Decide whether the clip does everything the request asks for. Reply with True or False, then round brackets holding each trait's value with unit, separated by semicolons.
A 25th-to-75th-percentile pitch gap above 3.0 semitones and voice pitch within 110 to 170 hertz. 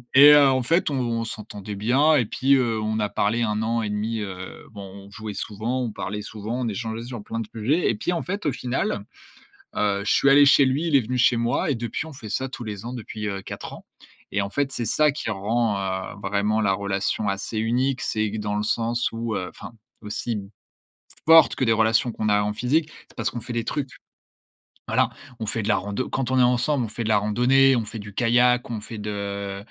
True (3.5 semitones; 115 Hz)